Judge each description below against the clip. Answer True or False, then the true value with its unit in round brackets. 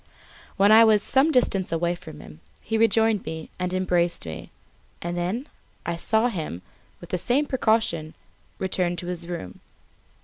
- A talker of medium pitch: True (180 Hz)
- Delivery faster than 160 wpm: False (150 wpm)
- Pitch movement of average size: True (4.6 semitones)